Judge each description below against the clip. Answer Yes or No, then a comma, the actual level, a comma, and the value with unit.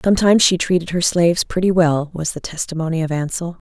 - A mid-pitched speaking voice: Yes, medium, 170 Hz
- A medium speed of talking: Yes, average, 195 wpm